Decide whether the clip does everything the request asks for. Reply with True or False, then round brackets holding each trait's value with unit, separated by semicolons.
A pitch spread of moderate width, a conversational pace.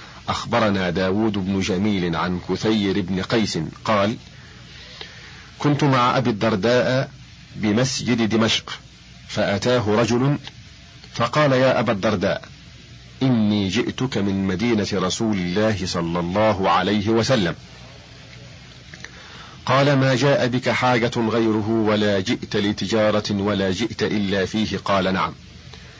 True (3.7 semitones; 105 wpm)